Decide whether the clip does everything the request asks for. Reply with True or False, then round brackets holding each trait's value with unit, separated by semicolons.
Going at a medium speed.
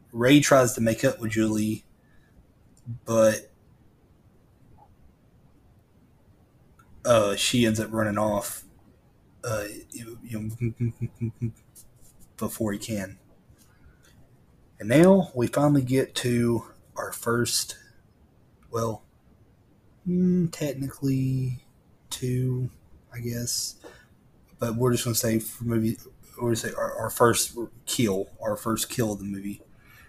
False (100 wpm)